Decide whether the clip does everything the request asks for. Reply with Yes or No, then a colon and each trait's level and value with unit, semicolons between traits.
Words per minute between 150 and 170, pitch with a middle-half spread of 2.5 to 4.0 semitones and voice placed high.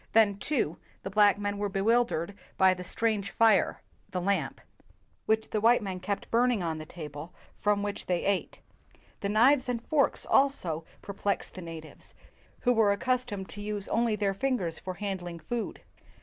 Yes: average, 165 wpm; average, 3.6 semitones; high, 205 Hz